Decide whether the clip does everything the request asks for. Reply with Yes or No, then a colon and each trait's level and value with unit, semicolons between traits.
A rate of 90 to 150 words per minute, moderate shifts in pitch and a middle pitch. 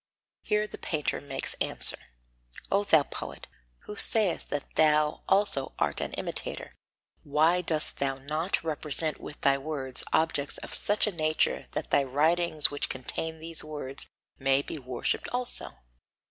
Yes: average, 145 wpm; average, 3.1 semitones; medium, 155 Hz